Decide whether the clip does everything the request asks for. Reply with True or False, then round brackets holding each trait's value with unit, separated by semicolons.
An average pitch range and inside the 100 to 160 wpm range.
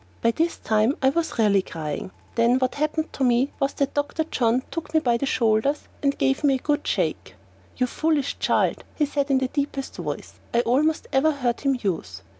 False (3.7 semitones; 205 wpm)